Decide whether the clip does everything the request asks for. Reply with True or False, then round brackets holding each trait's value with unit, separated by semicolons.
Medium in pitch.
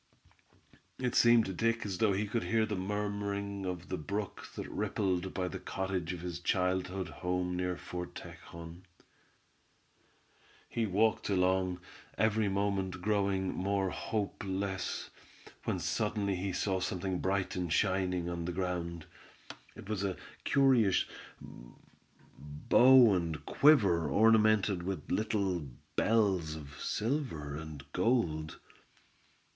False (95 Hz)